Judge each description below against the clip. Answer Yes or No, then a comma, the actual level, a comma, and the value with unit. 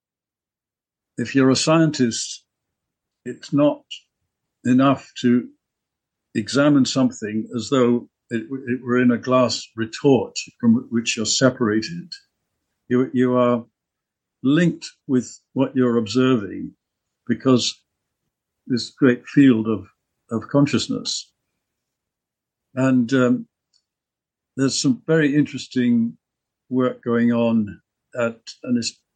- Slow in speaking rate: Yes, slow, 100 wpm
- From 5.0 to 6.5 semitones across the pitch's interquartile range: No, narrow, 2.4 semitones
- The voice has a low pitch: Yes, low, 125 Hz